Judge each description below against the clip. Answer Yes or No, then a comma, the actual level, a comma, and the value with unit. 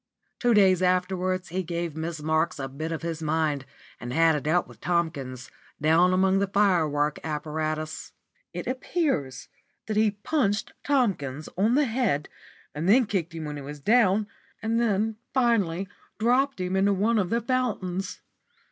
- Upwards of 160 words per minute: No, average, 155 wpm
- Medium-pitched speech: Yes, medium, 180 Hz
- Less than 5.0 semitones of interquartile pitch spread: No, average, 5.3 semitones